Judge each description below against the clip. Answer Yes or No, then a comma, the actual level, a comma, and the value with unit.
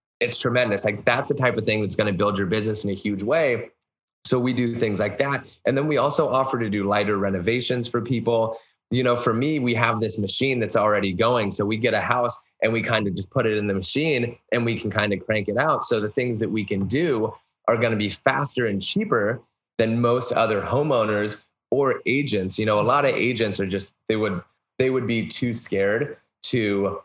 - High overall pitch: No, low, 110 Hz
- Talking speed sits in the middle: No, fast, 235 wpm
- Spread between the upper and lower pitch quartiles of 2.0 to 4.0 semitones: Yes, average, 2.7 semitones